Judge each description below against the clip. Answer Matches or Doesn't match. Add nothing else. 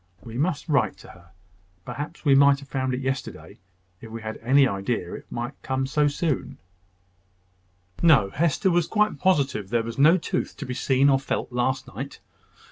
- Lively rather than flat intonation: Doesn't match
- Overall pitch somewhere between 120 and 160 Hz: Matches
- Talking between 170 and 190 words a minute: Matches